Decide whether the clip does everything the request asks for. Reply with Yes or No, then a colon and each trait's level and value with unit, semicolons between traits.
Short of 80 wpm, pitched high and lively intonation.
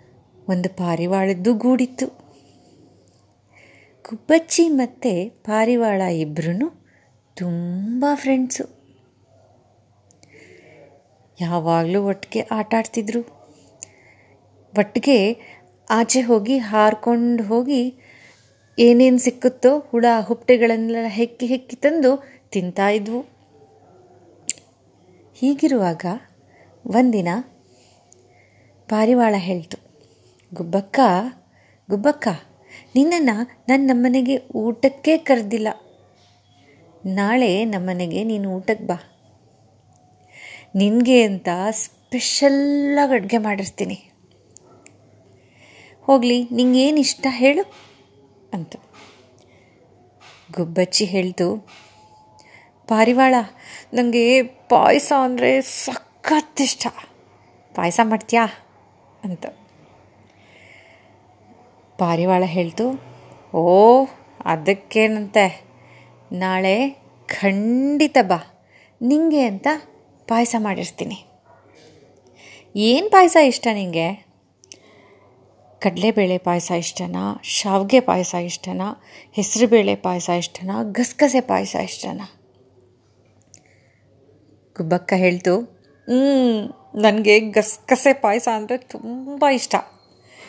Yes: slow, 65 wpm; high, 215 Hz; wide, 6.5 semitones